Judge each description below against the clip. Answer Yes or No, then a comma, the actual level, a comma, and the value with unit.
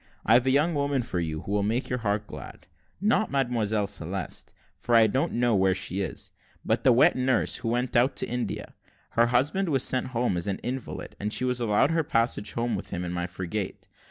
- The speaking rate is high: Yes, fast, 220 wpm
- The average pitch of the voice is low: Yes, low, 120 Hz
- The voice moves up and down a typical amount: Yes, average, 4.1 semitones